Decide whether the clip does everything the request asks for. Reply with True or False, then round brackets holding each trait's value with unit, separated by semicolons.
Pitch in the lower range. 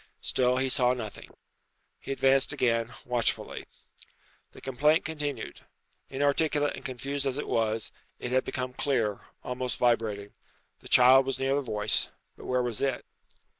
True (130 Hz)